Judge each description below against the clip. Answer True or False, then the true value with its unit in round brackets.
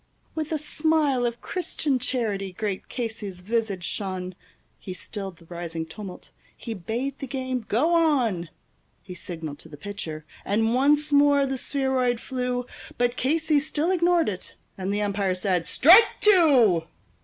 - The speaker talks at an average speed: True (150 wpm)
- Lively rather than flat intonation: True (7.0 semitones)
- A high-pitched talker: True (235 Hz)